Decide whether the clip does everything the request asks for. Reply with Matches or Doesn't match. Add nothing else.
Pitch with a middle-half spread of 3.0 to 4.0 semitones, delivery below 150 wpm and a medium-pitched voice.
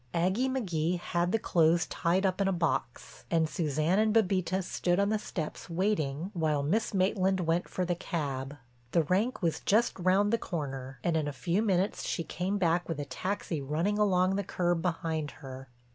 Doesn't match